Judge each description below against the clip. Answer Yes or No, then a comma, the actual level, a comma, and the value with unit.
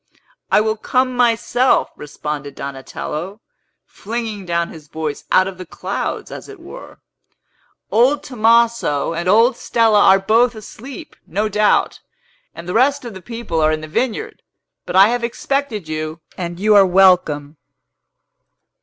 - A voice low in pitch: No, high, 210 Hz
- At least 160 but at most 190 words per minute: No, average, 145 wpm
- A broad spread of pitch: Yes, wide, 5.9 semitones